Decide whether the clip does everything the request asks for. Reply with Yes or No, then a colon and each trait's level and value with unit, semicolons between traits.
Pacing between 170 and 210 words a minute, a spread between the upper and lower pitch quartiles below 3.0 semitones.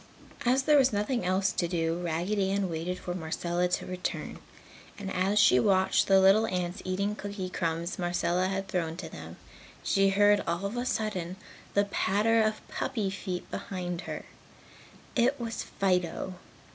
No: average, 160 wpm; narrow, 2.6 semitones